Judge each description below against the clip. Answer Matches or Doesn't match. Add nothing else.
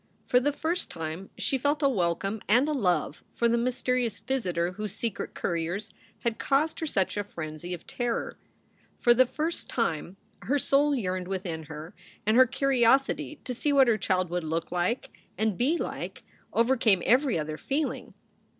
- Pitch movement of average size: Doesn't match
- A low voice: Doesn't match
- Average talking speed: Matches